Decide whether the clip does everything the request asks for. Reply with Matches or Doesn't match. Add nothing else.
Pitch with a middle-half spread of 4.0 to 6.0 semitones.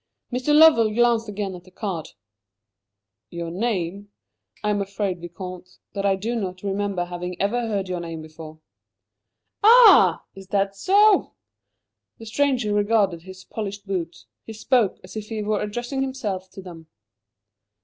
Doesn't match